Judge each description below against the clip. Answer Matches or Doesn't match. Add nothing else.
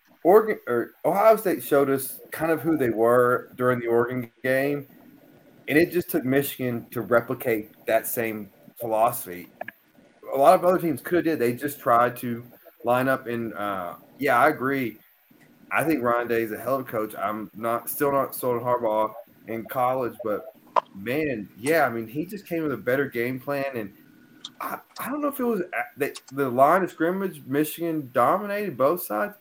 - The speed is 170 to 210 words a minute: Matches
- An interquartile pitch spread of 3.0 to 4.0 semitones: Doesn't match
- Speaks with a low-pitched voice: Matches